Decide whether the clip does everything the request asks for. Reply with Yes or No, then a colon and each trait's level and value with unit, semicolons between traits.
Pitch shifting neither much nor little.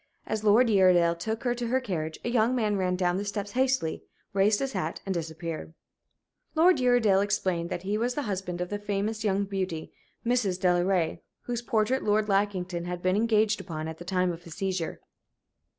Yes: average, 3.7 semitones